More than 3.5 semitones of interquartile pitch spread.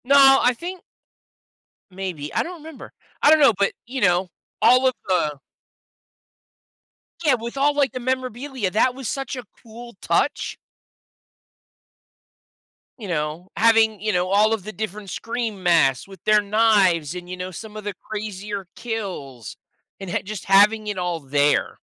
Yes: average, 5.1 semitones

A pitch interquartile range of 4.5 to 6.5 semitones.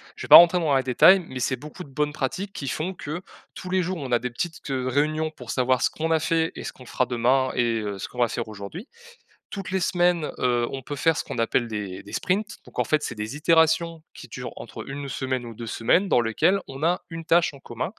Yes: average, 5.2 semitones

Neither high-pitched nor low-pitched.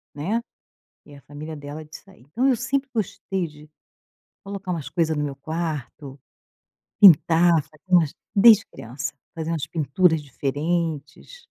Yes: medium, 160 Hz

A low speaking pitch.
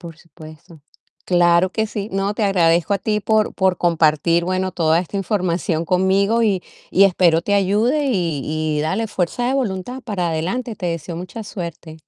No: medium, 185 Hz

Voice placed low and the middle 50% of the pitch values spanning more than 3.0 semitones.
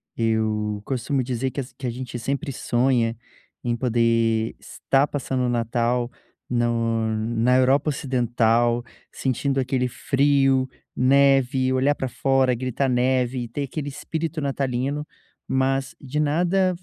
No: low, 130 Hz; narrow, 2.5 semitones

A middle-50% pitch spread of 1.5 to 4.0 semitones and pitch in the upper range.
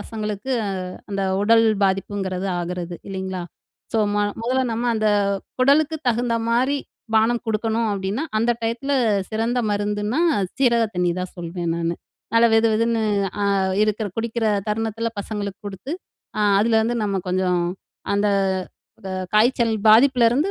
Yes: average, 3.0 semitones; high, 220 Hz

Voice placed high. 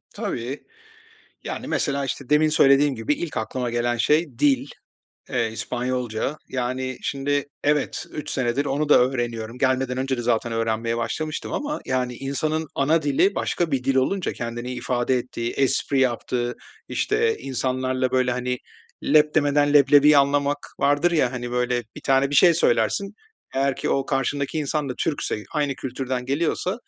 No: low, 135 Hz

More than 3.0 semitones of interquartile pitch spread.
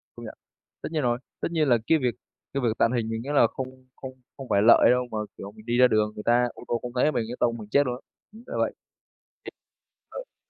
No: narrow, 2.4 semitones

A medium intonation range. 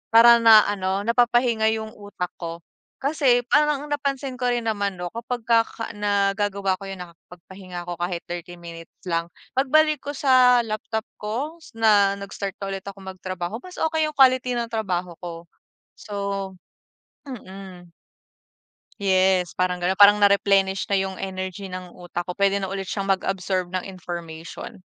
Yes: average, 4.1 semitones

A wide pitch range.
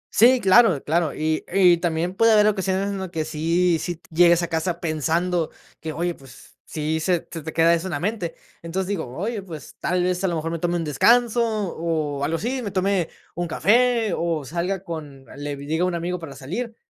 No: average, 3.1 semitones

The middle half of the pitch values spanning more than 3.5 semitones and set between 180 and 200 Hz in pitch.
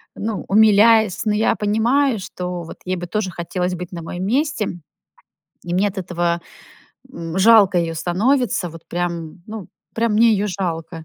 Yes: average, 4.0 semitones; medium, 185 Hz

